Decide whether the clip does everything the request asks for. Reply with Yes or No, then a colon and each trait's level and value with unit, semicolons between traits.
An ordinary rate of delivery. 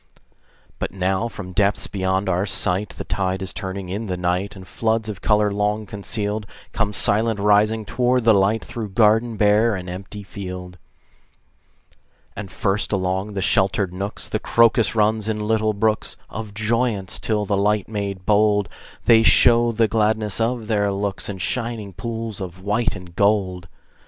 Yes: average, 160 wpm